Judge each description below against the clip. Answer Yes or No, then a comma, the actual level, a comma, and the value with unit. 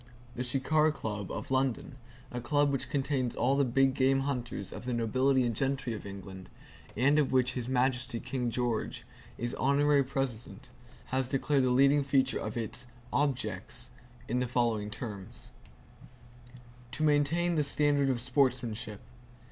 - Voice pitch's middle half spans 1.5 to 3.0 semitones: Yes, narrow, 2.6 semitones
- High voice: No, low, 130 Hz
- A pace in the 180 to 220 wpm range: No, average, 155 wpm